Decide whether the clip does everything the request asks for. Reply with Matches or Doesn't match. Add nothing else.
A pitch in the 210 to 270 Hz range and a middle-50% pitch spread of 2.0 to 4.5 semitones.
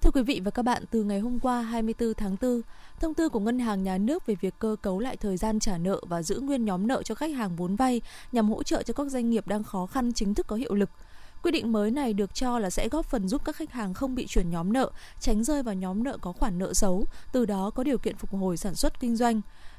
Matches